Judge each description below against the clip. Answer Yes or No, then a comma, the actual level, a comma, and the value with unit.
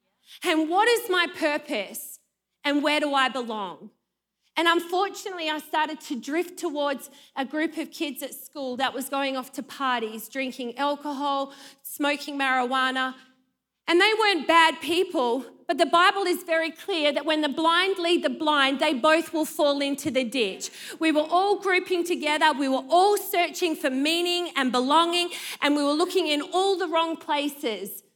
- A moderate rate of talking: Yes, average, 170 wpm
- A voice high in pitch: Yes, very high, 300 Hz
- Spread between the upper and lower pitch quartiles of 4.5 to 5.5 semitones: No, average, 4.0 semitones